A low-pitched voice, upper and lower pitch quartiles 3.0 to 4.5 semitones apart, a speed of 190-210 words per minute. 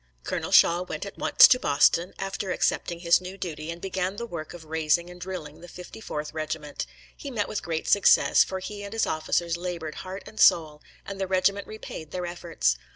No: medium, 175 Hz; average, 3.3 semitones; average, 200 wpm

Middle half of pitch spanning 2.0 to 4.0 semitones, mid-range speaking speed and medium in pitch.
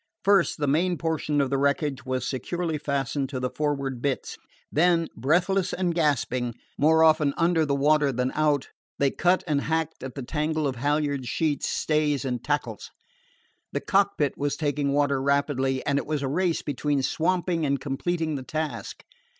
Yes: average, 2.7 semitones; average, 170 wpm; medium, 145 Hz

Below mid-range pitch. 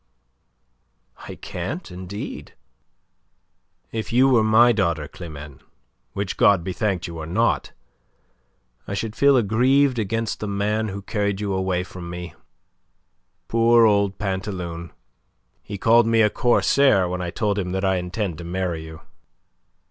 Yes: low, 100 Hz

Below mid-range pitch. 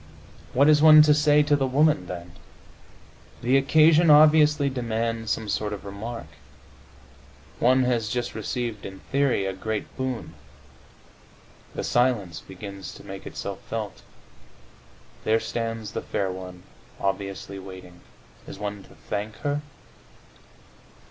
Yes: low, 115 Hz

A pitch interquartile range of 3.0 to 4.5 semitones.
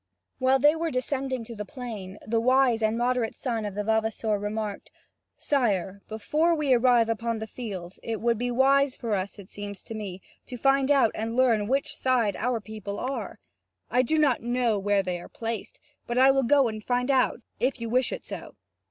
Yes: average, 3.3 semitones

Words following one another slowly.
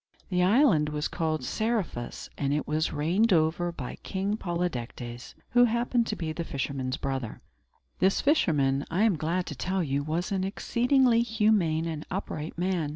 No: average, 160 wpm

